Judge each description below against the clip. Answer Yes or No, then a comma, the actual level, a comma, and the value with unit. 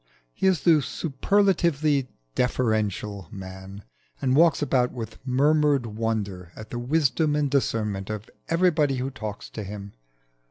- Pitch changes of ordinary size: No, wide, 5.9 semitones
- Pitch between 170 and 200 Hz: No, low, 125 Hz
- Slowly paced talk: Yes, slow, 130 wpm